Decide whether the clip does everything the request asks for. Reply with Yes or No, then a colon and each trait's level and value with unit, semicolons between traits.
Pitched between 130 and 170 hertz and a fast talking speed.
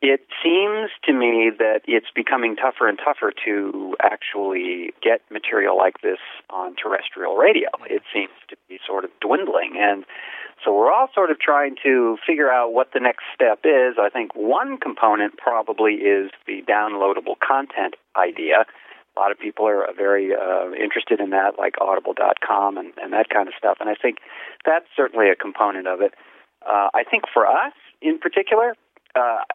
No: low, 135 Hz; average, 175 wpm